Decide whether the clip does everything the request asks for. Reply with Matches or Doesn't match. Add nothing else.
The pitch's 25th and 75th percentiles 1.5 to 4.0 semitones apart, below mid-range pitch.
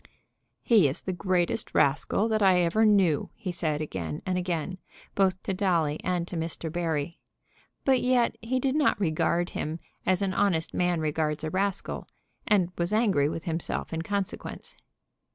Doesn't match